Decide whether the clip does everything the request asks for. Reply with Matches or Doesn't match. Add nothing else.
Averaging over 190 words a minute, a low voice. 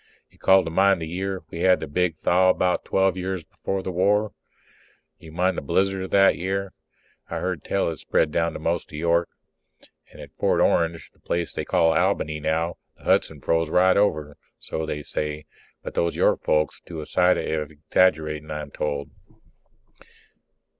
Doesn't match